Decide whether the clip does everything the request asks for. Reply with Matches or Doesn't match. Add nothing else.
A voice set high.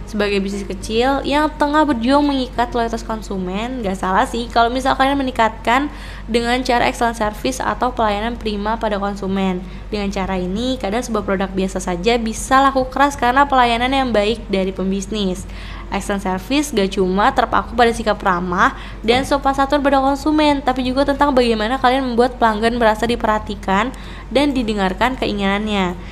Matches